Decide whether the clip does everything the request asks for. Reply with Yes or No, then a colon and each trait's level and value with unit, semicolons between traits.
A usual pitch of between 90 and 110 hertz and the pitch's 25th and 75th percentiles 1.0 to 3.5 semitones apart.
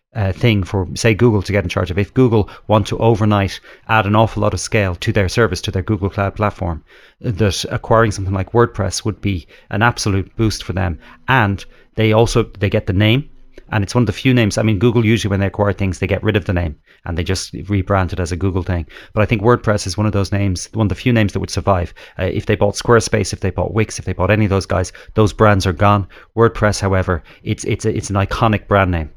Yes: low, 100 Hz; narrow, 2.6 semitones